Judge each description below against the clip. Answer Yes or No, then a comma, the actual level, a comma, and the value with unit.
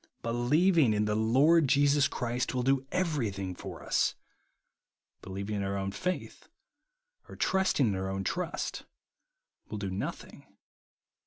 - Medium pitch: No, low, 120 Hz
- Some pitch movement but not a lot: No, wide, 6.8 semitones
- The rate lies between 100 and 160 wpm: Yes, average, 140 wpm